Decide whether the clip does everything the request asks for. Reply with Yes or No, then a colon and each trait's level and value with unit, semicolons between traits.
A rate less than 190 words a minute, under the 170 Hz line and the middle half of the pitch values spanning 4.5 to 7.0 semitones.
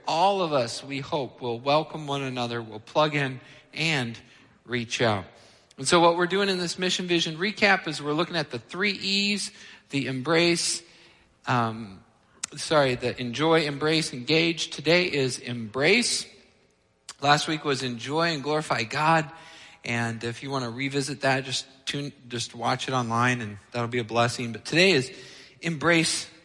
Yes: average, 165 wpm; medium, 140 Hz; average, 5.1 semitones